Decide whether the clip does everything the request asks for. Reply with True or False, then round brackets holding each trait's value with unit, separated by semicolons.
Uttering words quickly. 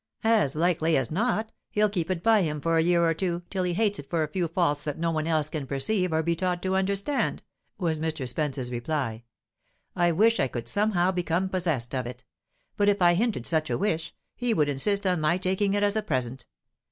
True (225 wpm)